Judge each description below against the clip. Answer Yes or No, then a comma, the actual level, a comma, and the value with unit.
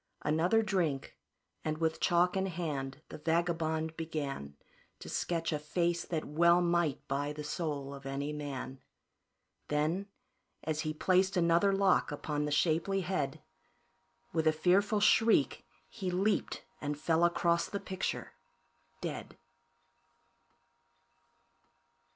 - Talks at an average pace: No, slow, 120 wpm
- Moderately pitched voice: Yes, medium, 160 Hz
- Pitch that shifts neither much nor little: Yes, average, 3.2 semitones